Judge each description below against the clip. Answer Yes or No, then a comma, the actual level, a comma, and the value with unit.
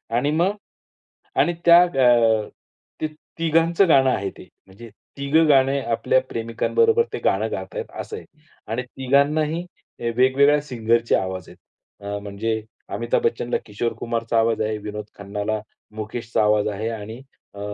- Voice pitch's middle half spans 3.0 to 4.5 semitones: No, average, 5.0 semitones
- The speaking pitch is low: Yes, low, 120 Hz